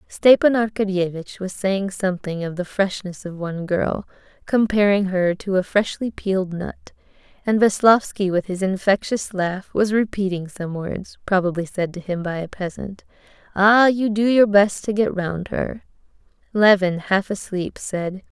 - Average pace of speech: Yes, average, 155 wpm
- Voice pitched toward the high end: Yes, high, 195 Hz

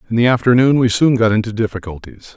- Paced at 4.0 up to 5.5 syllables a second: No, 6.6 syllables/s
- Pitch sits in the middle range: No, low, 115 Hz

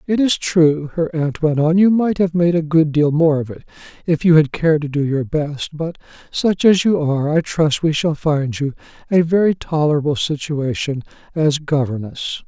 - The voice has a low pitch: No, medium, 155 Hz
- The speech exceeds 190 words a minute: Yes, average, 200 wpm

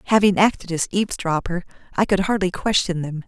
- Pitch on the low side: No, medium, 185 Hz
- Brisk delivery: No, average, 165 wpm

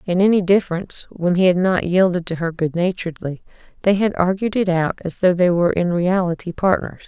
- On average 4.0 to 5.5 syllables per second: No, 5.7 syllables/s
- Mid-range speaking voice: Yes, medium, 180 Hz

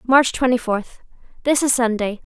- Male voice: No, female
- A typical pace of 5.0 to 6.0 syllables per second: No, 4.6 syllables/s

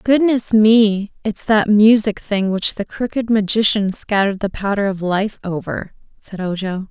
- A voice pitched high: Yes, high, 205 Hz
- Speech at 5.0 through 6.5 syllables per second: No, 4.4 syllables/s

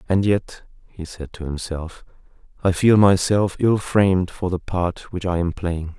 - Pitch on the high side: No, very low, 90 Hz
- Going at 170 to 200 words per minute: Yes, average, 180 wpm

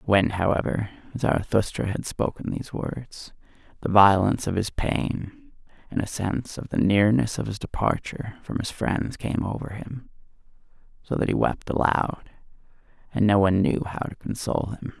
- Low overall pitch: Yes, low, 100 Hz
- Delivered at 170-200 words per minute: No, average, 160 wpm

